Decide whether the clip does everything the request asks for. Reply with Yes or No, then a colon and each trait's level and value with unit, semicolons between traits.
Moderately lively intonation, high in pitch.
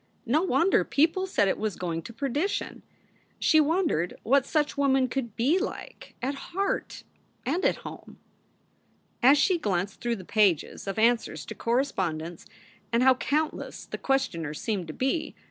No: wide, 7.0 semitones; very high, 255 Hz